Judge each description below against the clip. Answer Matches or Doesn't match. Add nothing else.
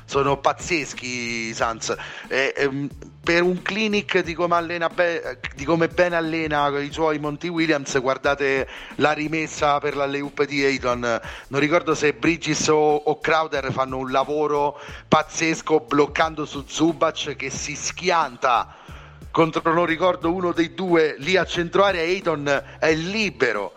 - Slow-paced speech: Doesn't match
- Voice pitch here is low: Doesn't match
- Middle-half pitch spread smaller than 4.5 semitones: Matches